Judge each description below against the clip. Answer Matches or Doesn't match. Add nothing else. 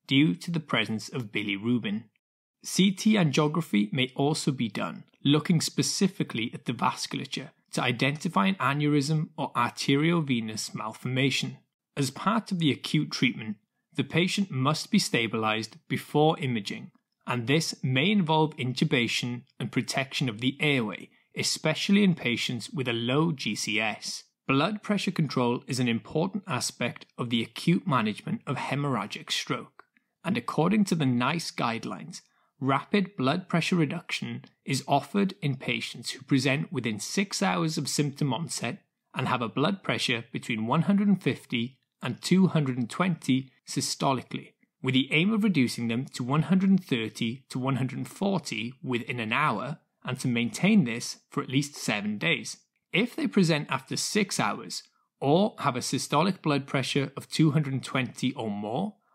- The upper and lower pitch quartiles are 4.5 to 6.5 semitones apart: Matches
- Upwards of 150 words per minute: Doesn't match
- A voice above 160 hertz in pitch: Doesn't match